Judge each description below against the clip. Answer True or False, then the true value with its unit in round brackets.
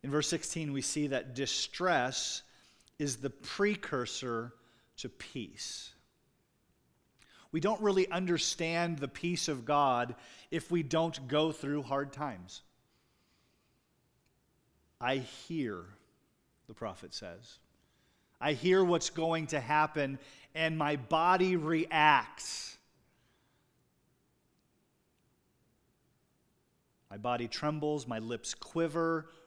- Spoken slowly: True (100 wpm)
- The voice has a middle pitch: True (150 Hz)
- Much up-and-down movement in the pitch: False (3.8 semitones)